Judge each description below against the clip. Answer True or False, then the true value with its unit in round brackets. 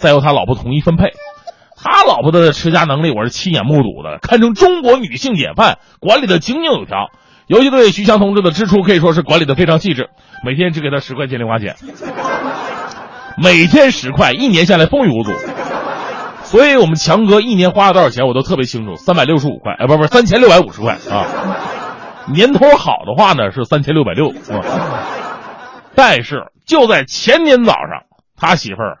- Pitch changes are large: True (6.7 semitones)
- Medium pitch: True (170 Hz)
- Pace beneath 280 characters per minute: False (295 characters per minute)